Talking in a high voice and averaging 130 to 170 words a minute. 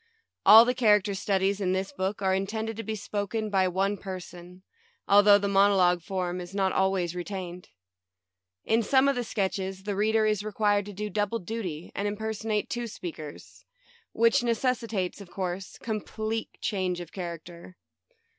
Yes: high, 200 Hz; average, 165 wpm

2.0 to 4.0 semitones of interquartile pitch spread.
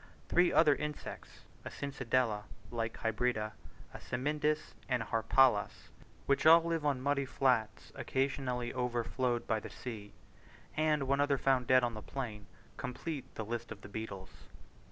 Yes: average, 3.7 semitones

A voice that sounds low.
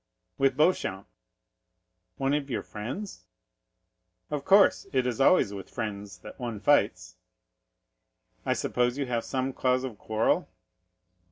Yes: low, 125 Hz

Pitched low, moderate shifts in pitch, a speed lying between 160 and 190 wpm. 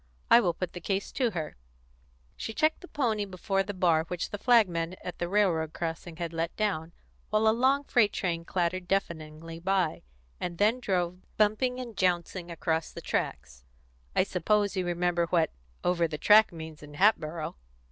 No: medium, 180 Hz; average, 3.8 semitones; average, 175 wpm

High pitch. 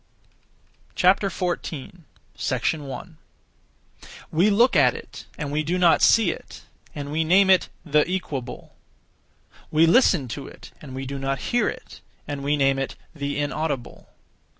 No: medium, 150 Hz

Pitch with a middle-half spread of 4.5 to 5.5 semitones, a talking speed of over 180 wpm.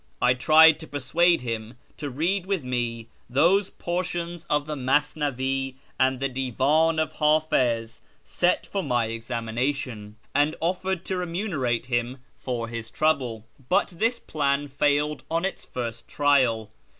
No: average, 4.9 semitones; average, 140 wpm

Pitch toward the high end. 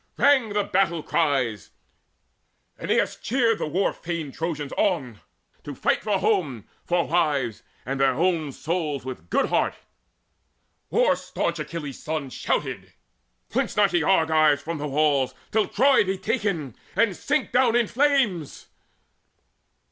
No: medium, 165 Hz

